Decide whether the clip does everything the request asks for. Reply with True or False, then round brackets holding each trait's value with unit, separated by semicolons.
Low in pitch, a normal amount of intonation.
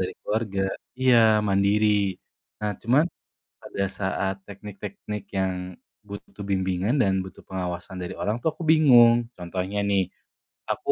False (100 Hz; 2.2 semitones)